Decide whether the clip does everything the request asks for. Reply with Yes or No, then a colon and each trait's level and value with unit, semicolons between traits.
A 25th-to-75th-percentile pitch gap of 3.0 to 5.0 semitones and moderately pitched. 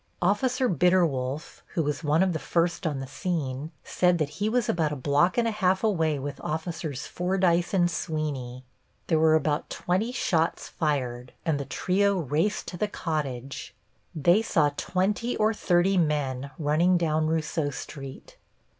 Yes: average, 4.0 semitones; medium, 160 Hz